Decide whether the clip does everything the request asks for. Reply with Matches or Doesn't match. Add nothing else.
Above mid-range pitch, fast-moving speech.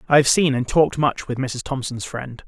Doesn't match